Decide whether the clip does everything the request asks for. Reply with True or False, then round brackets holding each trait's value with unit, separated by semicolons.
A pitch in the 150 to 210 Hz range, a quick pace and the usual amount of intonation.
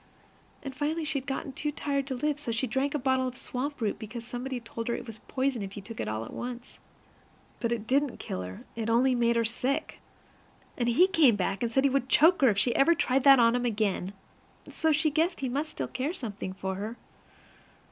False (250 Hz; 240 wpm; 3.5 semitones)